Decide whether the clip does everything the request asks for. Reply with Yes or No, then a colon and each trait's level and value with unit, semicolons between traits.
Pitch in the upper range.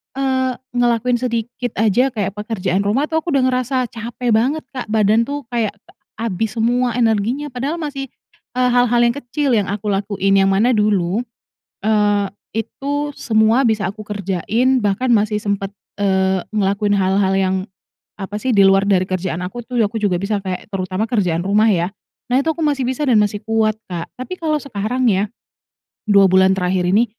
Yes: high, 220 Hz